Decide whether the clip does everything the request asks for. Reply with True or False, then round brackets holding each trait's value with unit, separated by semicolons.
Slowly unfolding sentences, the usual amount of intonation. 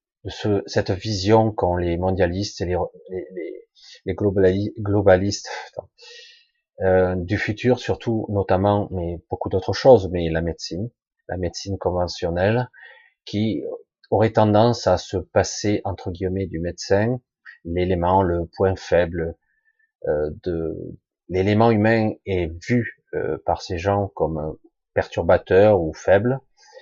True (120 wpm; 5.0 semitones)